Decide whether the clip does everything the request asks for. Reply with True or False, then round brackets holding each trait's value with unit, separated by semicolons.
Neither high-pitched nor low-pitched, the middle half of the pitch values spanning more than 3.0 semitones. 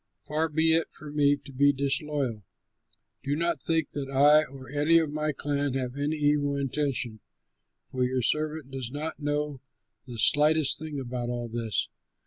False (145 Hz; 2.4 semitones)